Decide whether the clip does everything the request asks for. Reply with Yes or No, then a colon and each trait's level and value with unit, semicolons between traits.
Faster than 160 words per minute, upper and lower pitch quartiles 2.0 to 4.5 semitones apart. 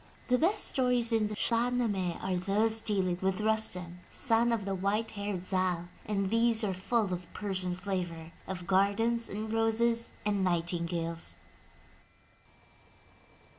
No: average, 140 wpm; average, 3.7 semitones